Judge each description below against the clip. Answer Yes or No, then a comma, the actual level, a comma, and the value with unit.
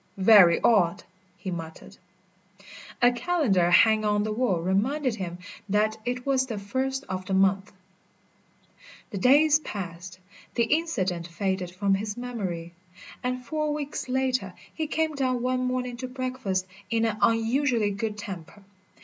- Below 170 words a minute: Yes, average, 140 wpm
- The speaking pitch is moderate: No, high, 220 Hz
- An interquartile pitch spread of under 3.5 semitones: No, average, 5.1 semitones